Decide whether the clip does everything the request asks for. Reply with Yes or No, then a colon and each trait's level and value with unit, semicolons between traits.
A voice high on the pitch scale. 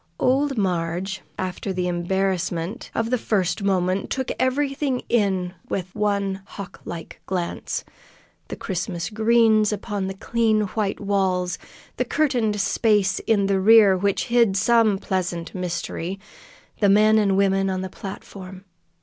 Yes: high, 195 Hz